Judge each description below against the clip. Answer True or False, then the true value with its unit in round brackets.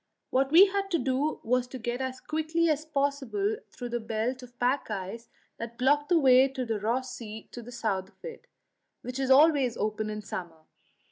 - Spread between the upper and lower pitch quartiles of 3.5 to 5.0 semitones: True (3.8 semitones)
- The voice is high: True (255 Hz)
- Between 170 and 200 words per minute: True (195 wpm)